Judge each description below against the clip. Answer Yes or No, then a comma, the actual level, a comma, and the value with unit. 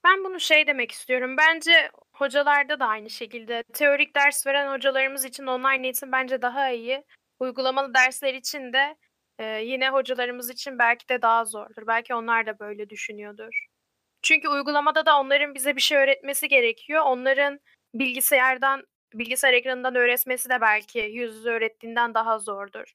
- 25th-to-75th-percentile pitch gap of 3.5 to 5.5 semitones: No, average, 3.1 semitones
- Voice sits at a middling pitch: No, very high, 260 Hz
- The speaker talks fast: Yes, fast, 150 wpm